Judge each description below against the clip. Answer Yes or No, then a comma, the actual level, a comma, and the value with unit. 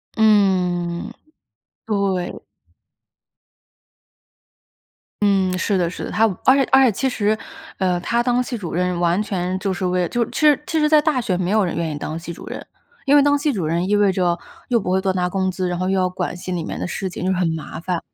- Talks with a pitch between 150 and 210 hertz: Yes, high, 190 Hz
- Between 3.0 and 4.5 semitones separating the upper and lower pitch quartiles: Yes, average, 3.6 semitones